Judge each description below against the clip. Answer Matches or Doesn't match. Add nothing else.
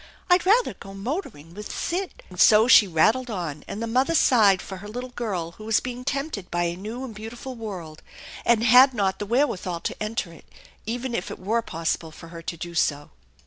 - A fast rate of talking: Matches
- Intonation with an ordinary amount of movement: Doesn't match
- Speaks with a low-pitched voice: Doesn't match